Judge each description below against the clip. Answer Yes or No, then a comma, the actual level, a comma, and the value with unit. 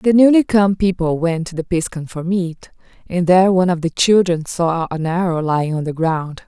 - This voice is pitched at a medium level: Yes, medium, 175 Hz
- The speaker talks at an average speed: No, fast, 215 wpm